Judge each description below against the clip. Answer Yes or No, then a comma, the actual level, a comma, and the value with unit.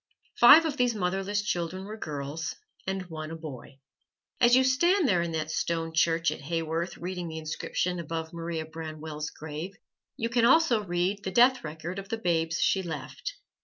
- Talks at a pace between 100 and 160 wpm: No, average, 175 wpm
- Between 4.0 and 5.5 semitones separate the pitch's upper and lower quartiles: Yes, average, 4.4 semitones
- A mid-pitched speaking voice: Yes, medium, 170 Hz